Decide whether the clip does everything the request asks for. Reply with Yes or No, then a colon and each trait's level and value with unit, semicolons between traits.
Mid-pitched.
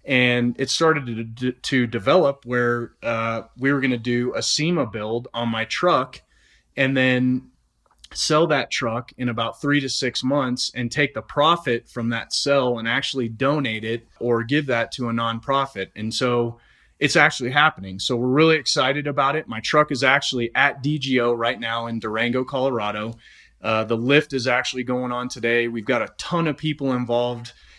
No: low, 125 Hz